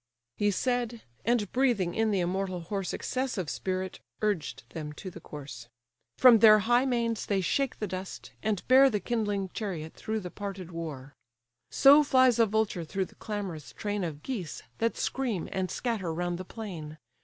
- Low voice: No, high, 200 Hz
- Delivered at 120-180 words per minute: Yes, average, 170 wpm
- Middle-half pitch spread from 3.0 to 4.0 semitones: No, average, 4.6 semitones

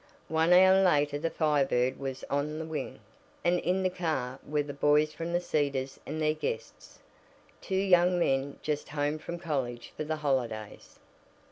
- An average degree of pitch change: Yes, average, 3.5 semitones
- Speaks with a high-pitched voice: No, medium, 150 Hz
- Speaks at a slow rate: No, average, 170 wpm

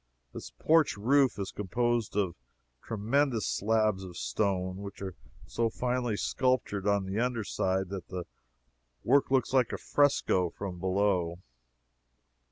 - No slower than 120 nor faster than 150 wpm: Yes, slow, 135 wpm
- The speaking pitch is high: No, low, 105 Hz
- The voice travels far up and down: No, average, 4.4 semitones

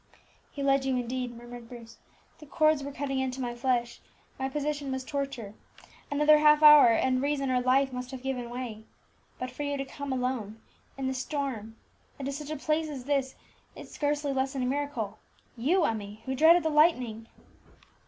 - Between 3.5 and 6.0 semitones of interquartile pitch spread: No, average, 2.8 semitones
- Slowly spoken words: No, average, 185 wpm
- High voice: Yes, very high, 265 Hz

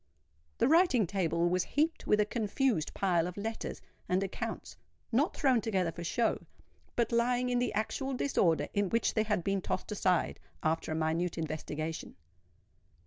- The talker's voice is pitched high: Yes, high, 200 Hz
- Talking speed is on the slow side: No, average, 155 wpm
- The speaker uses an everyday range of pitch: No, wide, 5.8 semitones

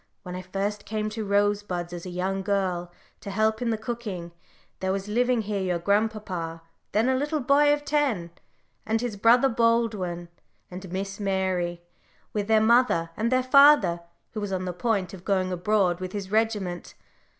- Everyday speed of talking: Yes, average, 175 wpm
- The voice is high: Yes, high, 205 Hz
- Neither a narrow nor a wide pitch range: Yes, average, 3.6 semitones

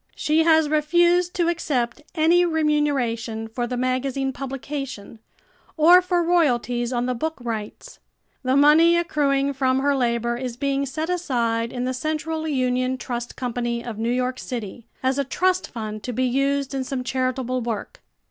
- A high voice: Yes, very high, 265 Hz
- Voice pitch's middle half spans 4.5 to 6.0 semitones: No, average, 4.1 semitones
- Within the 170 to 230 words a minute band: No, average, 160 wpm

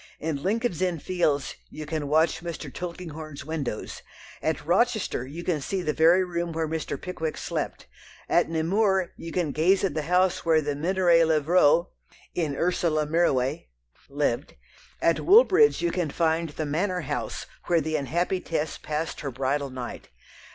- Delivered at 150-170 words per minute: Yes, average, 160 wpm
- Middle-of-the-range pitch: Yes, medium, 160 Hz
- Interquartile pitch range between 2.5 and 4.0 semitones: Yes, average, 2.9 semitones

